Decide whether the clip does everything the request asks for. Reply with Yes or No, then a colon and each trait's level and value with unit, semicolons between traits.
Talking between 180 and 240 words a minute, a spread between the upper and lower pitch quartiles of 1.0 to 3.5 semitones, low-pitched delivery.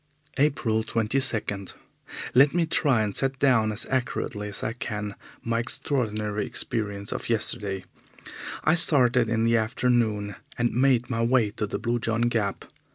No: average, 150 wpm; average, 2.9 semitones; low, 115 Hz